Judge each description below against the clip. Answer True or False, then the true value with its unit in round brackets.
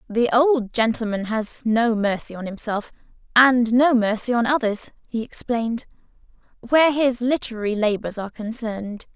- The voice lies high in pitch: True (230 Hz)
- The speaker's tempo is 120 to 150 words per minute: True (140 wpm)